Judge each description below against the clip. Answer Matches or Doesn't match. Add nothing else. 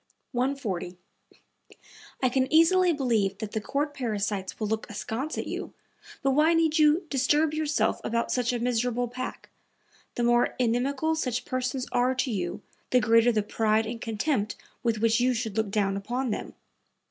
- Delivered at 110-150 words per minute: Doesn't match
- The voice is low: Doesn't match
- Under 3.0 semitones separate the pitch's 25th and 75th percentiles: Doesn't match